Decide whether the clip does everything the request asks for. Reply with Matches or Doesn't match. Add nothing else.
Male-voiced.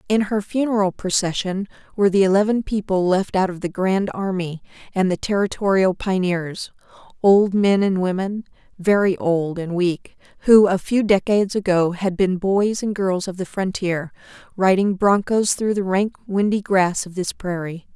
Doesn't match